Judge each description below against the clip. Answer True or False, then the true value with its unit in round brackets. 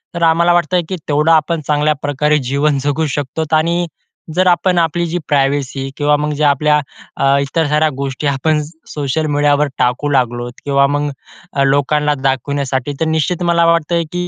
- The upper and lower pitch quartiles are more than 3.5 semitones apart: False (2.5 semitones)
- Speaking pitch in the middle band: True (150 Hz)